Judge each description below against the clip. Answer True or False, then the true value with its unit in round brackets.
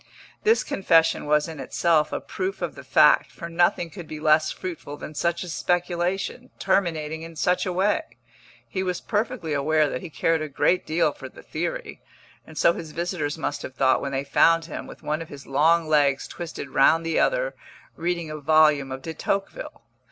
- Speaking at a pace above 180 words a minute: True (195 wpm)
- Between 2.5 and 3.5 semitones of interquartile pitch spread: True (2.8 semitones)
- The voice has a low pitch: False (165 Hz)